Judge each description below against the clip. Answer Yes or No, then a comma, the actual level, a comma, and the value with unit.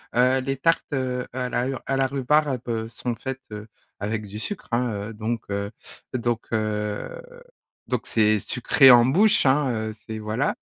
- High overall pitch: No, low, 120 Hz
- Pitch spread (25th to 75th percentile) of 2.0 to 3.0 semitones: No, average, 3.5 semitones